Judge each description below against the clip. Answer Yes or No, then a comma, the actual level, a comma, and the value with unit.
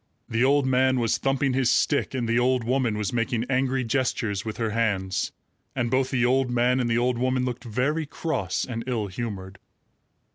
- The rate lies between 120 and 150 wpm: No, average, 190 wpm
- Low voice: Yes, low, 125 Hz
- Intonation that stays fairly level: Yes, narrow, 2.3 semitones